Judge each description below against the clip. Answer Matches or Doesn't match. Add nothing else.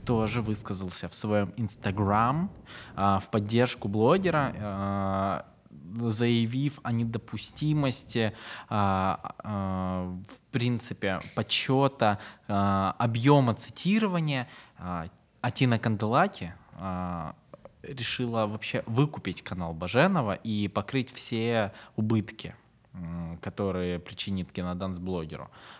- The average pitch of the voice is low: Matches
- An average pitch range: Matches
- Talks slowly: Matches